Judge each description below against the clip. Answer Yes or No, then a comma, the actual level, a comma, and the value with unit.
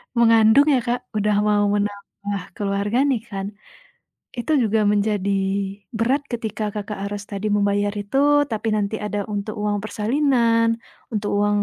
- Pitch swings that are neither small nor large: No, narrow, 2.1 semitones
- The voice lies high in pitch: Yes, high, 210 Hz